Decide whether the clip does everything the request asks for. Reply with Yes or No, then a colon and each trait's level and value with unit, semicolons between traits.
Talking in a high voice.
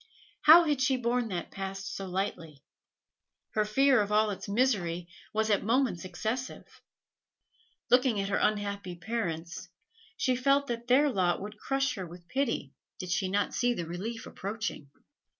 Yes: high, 210 Hz